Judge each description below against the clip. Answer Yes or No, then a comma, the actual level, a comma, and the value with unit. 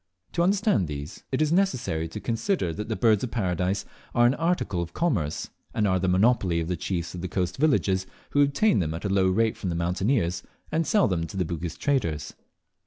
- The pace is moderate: No, fast, 215 wpm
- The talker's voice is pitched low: Yes, very low, 95 Hz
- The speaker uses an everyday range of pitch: No, wide, 7.5 semitones